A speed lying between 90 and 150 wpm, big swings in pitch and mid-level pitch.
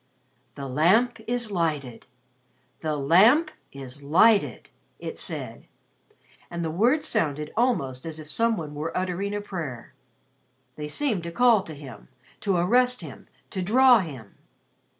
Yes: average, 140 wpm; wide, 7.3 semitones; medium, 170 Hz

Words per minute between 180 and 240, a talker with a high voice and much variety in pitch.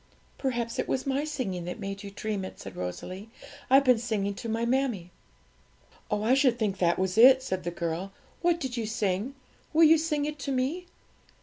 Yes: average, 200 wpm; high, 230 Hz; wide, 5.7 semitones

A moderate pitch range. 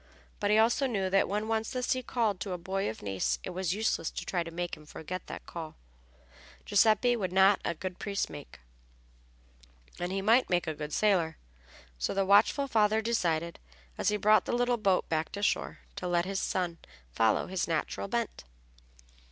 Yes: average, 4.9 semitones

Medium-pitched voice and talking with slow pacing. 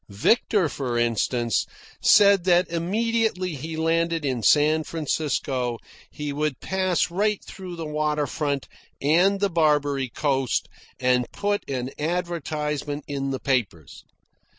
Yes: medium, 150 Hz; slow, 125 wpm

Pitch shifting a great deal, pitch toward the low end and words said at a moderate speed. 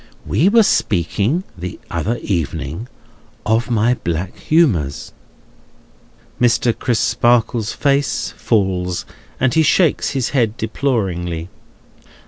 No: wide, 6.5 semitones; low, 110 Hz; slow, 100 wpm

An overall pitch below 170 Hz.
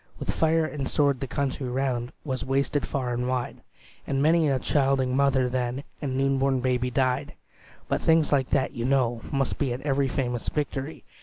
Yes: low, 135 Hz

